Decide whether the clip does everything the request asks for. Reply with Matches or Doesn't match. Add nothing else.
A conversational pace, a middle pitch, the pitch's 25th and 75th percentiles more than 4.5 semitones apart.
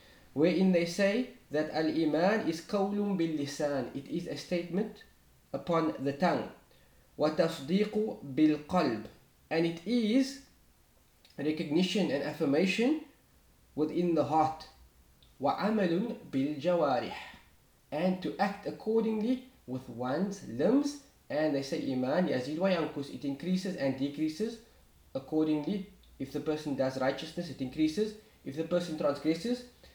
Doesn't match